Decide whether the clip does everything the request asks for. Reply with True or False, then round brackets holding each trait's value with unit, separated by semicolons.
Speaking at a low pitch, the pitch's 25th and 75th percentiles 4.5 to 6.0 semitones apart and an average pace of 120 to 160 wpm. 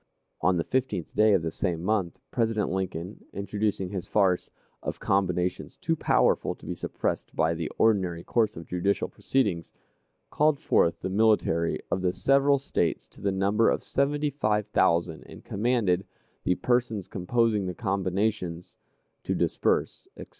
False (100 Hz; 4.0 semitones; 155 wpm)